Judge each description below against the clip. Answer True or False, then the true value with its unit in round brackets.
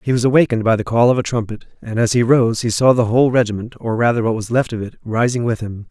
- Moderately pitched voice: False (115 Hz)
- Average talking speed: False (285 wpm)